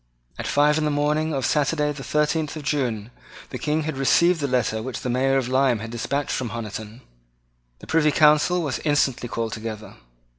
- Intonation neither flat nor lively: Yes, average, 4.0 semitones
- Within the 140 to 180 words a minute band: No, average, 190 wpm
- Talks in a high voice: No, medium, 140 Hz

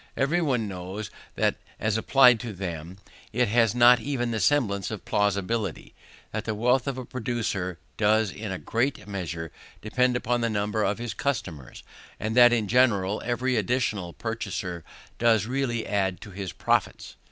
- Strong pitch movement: No, average, 3.7 semitones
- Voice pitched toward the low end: Yes, low, 110 Hz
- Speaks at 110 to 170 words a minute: Yes, average, 165 wpm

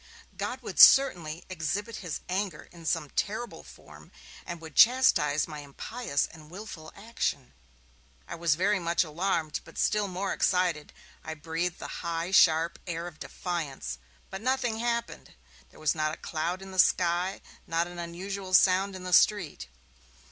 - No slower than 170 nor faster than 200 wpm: No, average, 155 wpm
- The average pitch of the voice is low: No, medium, 175 Hz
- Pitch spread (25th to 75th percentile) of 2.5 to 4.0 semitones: Yes, average, 3.5 semitones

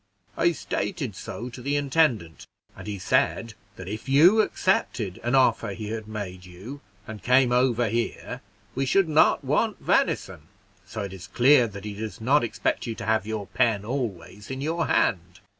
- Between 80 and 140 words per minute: No, average, 175 wpm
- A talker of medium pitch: No, low, 115 Hz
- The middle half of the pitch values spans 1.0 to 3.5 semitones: No, average, 4.8 semitones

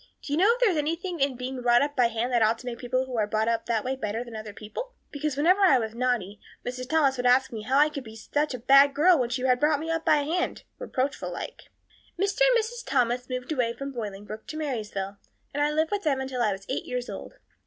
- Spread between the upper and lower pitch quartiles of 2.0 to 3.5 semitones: No, average, 4.3 semitones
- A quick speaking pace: Yes, fast, 260 wpm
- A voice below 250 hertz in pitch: No, very high, 260 Hz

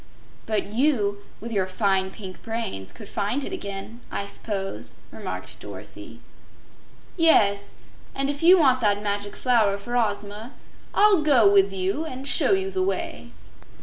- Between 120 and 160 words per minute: Yes, average, 150 wpm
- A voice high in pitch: Yes, high, 215 Hz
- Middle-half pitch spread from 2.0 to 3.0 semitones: No, average, 5.3 semitones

